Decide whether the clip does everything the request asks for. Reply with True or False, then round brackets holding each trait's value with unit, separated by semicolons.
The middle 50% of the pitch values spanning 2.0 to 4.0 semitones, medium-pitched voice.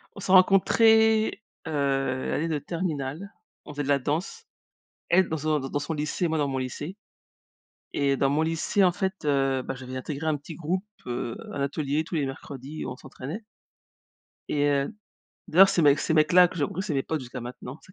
False (4.4 semitones; 150 Hz)